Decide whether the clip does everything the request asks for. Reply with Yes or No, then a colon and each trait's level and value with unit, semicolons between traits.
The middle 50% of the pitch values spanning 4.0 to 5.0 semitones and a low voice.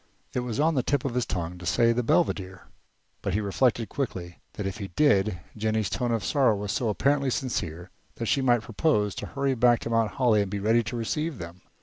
Yes: average, 4.5 semitones; low, 115 Hz